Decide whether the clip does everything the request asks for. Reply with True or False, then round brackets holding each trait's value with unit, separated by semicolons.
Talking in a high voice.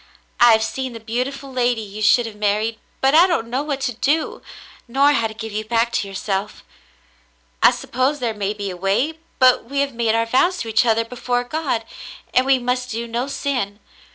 True (235 Hz)